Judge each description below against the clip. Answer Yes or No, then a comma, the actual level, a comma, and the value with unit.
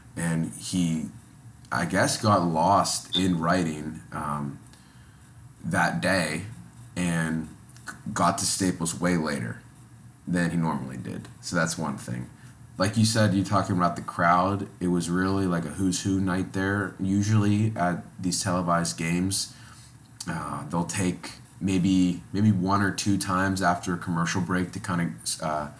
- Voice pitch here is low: Yes, very low, 90 Hz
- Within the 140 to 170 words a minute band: Yes, average, 150 wpm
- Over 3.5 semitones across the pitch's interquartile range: No, narrow, 2.4 semitones